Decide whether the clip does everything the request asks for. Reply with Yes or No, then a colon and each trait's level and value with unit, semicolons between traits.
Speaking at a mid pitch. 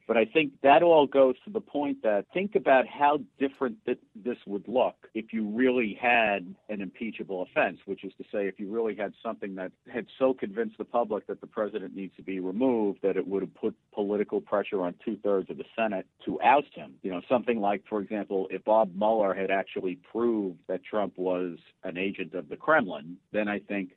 No: low, 105 Hz